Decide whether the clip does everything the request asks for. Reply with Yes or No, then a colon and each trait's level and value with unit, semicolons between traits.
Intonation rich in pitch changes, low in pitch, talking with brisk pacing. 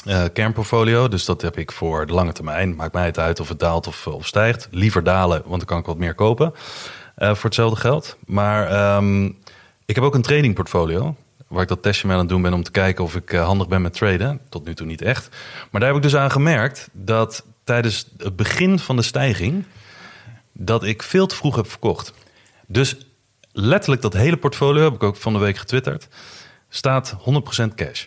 Yes: wide, 5.8 semitones; low, 110 Hz; fast, 215 wpm